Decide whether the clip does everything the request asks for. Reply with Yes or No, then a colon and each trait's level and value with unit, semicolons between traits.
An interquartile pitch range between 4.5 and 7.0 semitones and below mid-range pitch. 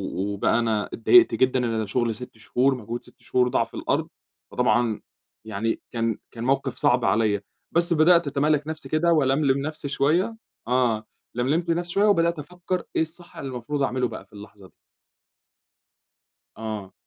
Yes: wide, 5.5 semitones; low, 130 Hz